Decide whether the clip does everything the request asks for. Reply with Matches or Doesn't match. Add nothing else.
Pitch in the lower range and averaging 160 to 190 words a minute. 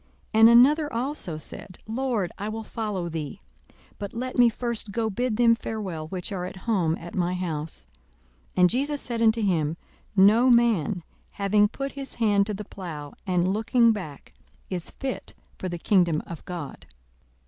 Doesn't match